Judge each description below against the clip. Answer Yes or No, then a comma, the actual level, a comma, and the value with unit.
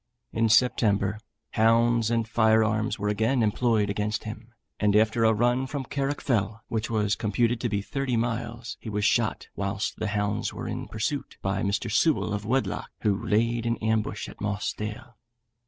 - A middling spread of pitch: No, narrow, 2.1 semitones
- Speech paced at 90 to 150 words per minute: No, average, 170 wpm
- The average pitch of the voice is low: Yes, low, 110 Hz